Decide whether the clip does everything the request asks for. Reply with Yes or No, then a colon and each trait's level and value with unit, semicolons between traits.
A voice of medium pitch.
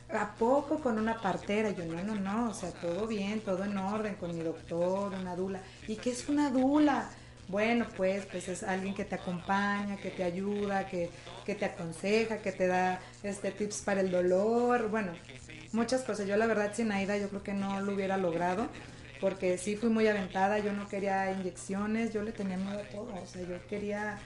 No: high, 200 Hz